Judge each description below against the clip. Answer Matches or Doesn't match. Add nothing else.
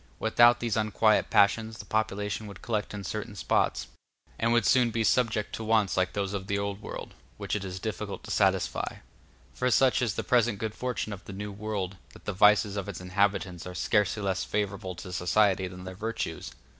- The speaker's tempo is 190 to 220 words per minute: Matches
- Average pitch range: Doesn't match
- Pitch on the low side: Matches